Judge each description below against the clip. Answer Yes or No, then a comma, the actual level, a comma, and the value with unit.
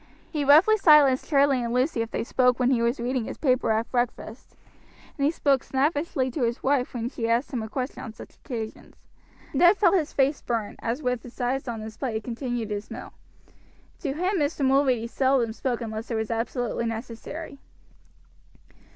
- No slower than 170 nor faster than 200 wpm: Yes, average, 190 wpm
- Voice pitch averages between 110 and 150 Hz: No, very high, 250 Hz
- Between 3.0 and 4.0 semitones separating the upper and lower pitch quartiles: Yes, average, 3.3 semitones